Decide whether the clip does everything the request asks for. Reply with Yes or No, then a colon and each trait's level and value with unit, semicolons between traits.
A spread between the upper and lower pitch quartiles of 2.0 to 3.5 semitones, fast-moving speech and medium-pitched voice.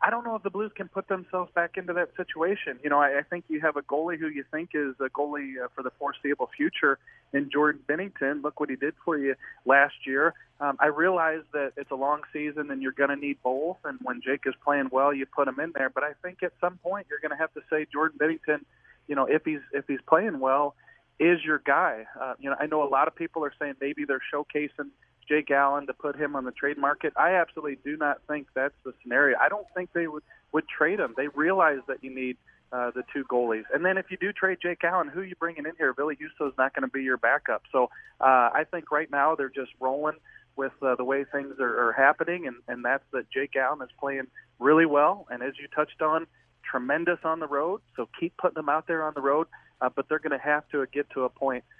Yes: average, 2.8 semitones; fast, 255 wpm; medium, 145 Hz